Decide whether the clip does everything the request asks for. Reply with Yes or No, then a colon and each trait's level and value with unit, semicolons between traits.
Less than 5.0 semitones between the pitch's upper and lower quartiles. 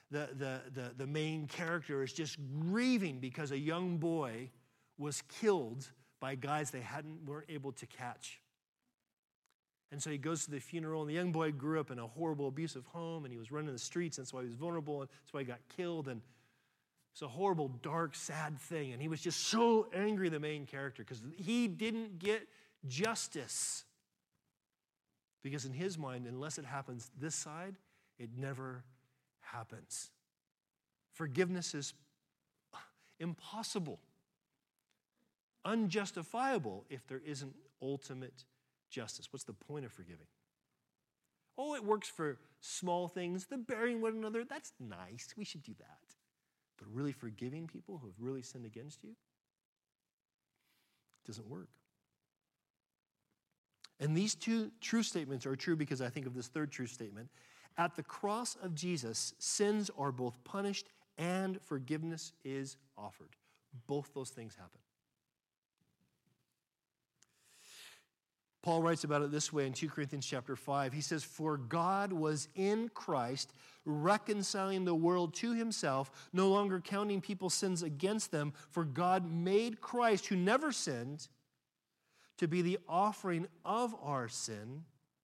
No: wide, 5.4 semitones